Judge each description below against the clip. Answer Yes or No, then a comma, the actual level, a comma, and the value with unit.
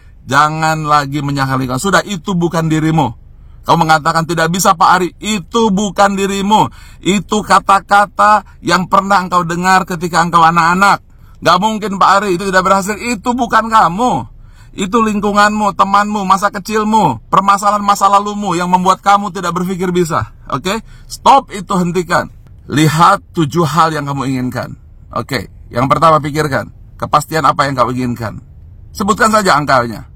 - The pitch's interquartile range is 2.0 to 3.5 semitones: No, average, 5.2 semitones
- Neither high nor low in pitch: Yes, medium, 180 Hz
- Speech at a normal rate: No, fast, 145 wpm